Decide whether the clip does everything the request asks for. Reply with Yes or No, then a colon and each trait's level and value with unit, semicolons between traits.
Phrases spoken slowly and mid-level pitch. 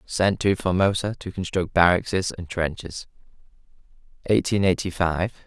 No: slow, 120 wpm; very low, 90 Hz